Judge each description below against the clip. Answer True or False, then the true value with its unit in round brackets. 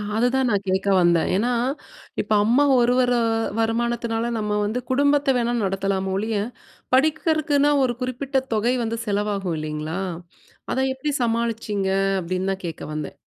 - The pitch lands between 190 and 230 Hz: True (225 Hz)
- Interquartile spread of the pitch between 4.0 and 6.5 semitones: True (4.7 semitones)